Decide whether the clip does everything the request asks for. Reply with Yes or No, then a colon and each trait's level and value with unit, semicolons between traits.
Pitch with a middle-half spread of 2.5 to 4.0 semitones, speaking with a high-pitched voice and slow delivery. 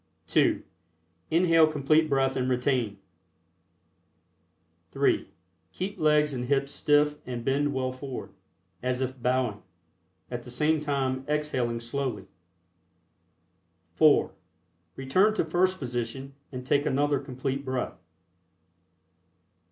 No: average, 2.9 semitones; low, 135 Hz; slow, 105 wpm